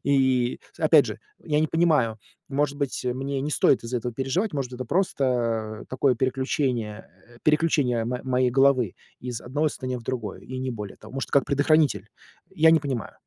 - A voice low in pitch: Yes, low, 130 Hz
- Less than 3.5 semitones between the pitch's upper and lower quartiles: Yes, average, 2.8 semitones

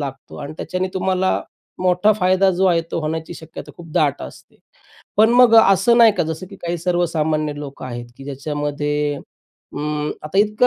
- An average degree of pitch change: Yes, average, 4.2 semitones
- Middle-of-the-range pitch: Yes, medium, 165 Hz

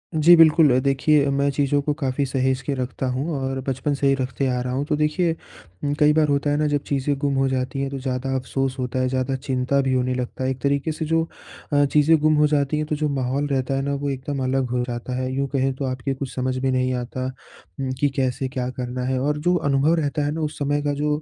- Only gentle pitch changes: Yes, narrow, 2.1 semitones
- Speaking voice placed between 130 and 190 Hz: Yes, low, 135 Hz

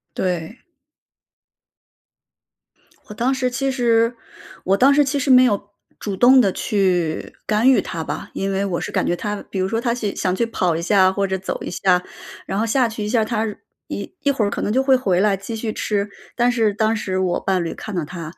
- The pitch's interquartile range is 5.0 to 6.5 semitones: No, average, 4.2 semitones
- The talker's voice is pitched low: No, high, 210 Hz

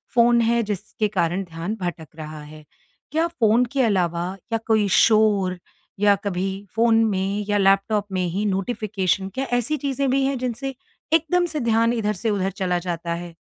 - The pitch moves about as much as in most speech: Yes, average, 4.2 semitones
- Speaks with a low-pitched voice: No, high, 205 Hz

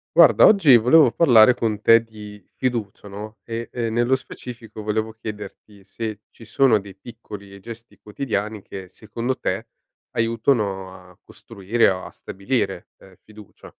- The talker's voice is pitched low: Yes, low, 110 Hz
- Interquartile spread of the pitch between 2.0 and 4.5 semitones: Yes, narrow, 2.5 semitones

